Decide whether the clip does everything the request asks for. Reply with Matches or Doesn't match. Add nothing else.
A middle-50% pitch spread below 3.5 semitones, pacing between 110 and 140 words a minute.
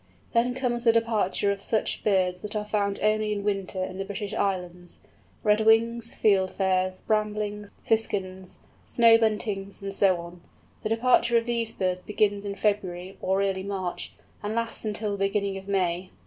Doesn't match